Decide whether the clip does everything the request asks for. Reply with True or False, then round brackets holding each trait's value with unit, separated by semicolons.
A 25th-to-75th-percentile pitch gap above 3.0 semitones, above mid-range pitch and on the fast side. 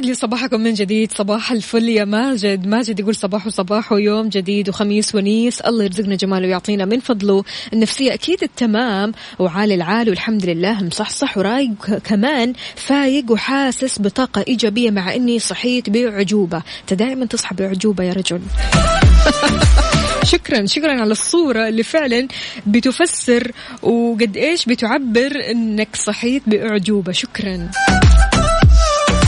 False (3.4 semitones; 220 Hz; 125 wpm)